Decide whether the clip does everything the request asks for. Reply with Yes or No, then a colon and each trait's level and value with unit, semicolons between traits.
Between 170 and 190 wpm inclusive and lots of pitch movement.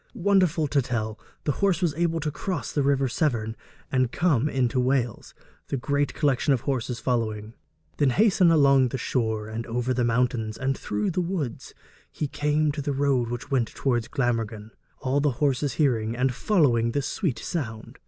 No: average, 175 wpm; average, 4.0 semitones